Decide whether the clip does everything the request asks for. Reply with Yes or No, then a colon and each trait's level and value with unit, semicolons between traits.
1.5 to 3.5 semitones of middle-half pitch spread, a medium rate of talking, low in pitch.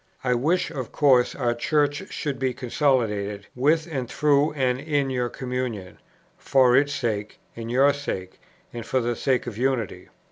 Yes: average, 3.1 semitones; average, 165 wpm; low, 130 Hz